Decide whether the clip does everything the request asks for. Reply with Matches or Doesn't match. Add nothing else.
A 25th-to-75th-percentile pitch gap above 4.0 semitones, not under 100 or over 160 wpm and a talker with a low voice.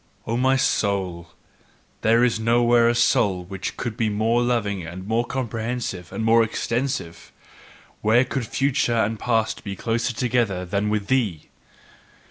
Doesn't match